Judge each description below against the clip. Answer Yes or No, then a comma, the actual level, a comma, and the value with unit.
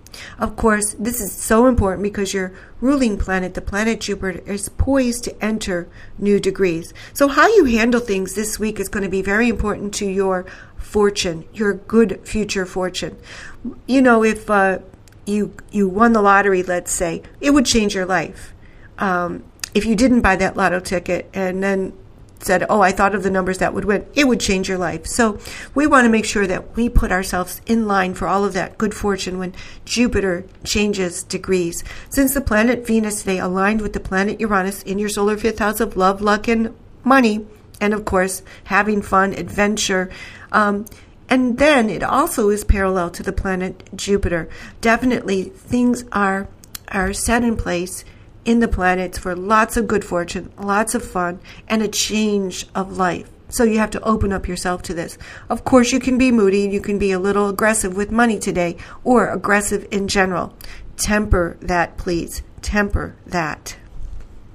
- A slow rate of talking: No, average, 180 wpm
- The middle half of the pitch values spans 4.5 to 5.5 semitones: No, average, 3.0 semitones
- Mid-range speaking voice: No, high, 200 Hz